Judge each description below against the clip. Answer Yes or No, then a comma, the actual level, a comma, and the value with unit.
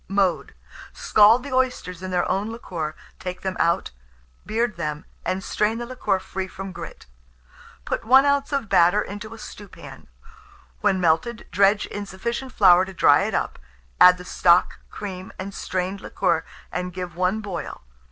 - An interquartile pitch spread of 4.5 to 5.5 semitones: No, average, 3.2 semitones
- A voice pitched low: No, high, 195 Hz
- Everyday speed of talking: Yes, average, 160 wpm